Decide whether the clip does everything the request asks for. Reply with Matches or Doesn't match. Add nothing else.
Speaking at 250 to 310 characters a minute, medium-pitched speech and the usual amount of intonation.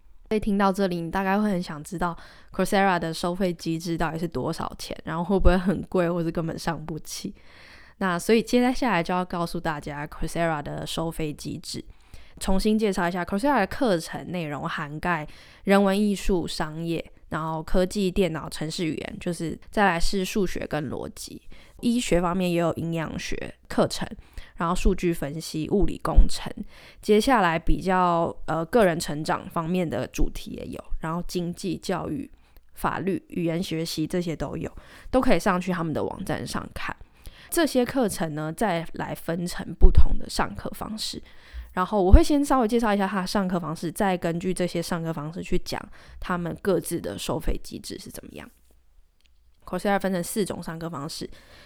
Matches